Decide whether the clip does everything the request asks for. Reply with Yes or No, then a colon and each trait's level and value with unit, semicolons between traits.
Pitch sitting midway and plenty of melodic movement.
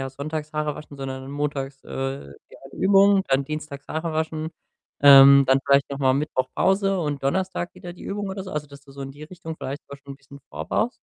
No: medium, 145 Hz; average, 2.9 semitones